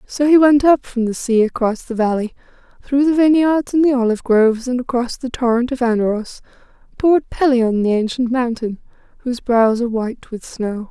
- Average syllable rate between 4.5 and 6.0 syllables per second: Yes, 5.5 syllables/s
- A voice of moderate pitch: No, high, 245 Hz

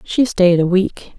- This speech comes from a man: No, female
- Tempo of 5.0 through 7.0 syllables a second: No, 3.7 syllables/s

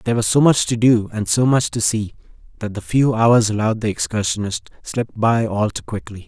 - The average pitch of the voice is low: Yes, low, 110 Hz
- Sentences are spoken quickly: Yes, fast, 220 wpm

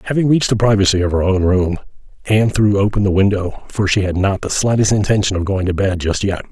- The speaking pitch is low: Yes, low, 100 Hz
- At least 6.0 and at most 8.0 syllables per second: Yes, 6.2 syllables/s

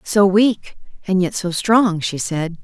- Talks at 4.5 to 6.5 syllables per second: No, 3.6 syllables/s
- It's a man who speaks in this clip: No, female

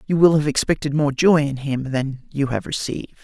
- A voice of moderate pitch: Yes, medium, 145 Hz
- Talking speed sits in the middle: No, fast, 225 wpm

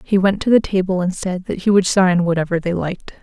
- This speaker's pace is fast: Yes, fast, 260 wpm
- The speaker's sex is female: Yes, female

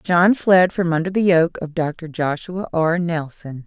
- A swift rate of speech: No, average, 180 wpm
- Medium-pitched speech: Yes, medium, 170 Hz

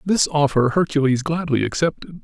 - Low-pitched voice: No, medium, 150 Hz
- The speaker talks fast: No, slow, 135 wpm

